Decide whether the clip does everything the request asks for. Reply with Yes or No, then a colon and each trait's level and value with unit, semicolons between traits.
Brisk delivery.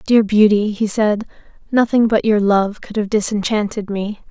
No: average, 165 wpm